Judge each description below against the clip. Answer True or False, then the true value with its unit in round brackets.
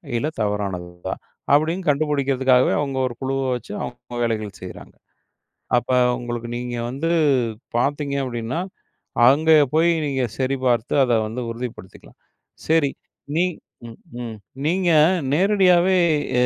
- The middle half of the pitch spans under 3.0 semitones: False (4.1 semitones)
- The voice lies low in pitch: True (130 Hz)